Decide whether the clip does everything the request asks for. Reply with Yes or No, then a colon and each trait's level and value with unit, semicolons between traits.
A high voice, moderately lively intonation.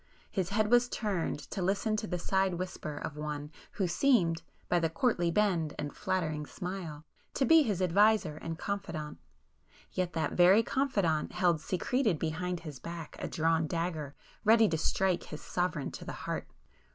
No: medium, 175 Hz; average, 4.0 semitones